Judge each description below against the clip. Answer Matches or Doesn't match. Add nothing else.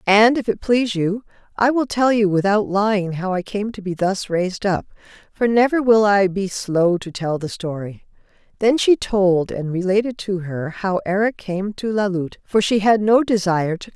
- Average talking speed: Doesn't match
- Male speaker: Doesn't match